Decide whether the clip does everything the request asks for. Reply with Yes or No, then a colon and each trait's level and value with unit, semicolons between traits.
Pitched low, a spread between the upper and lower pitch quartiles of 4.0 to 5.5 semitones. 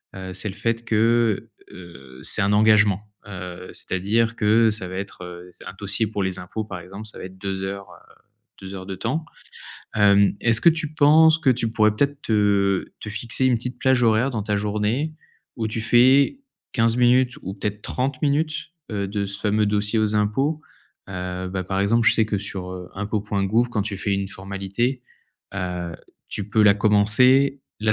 No: low, 105 Hz; average, 3.3 semitones